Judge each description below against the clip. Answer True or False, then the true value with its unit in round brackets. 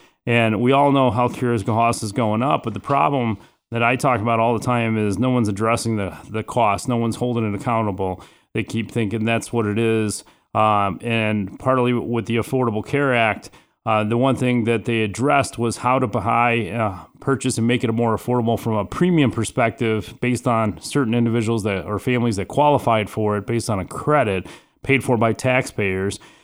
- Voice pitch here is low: True (115 Hz)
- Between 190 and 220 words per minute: True (200 wpm)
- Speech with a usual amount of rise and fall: False (2.2 semitones)